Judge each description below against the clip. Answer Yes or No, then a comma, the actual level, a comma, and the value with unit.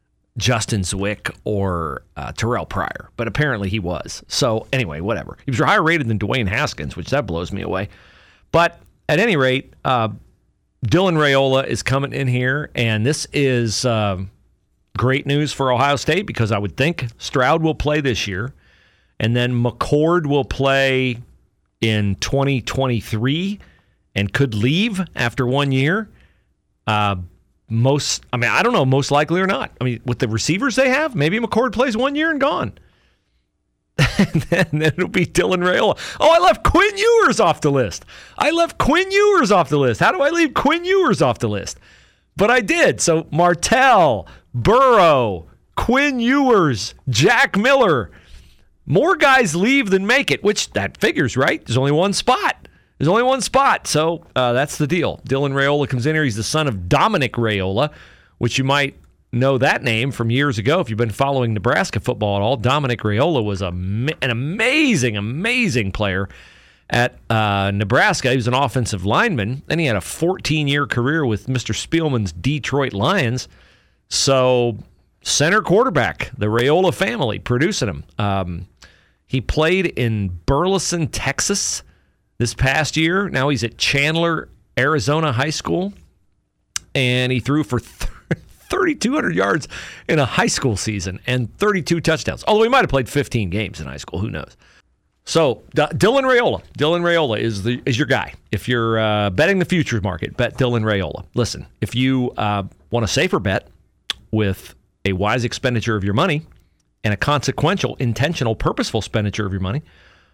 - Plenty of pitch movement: Yes, wide, 7.0 semitones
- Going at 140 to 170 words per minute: Yes, average, 165 wpm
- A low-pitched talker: Yes, low, 130 Hz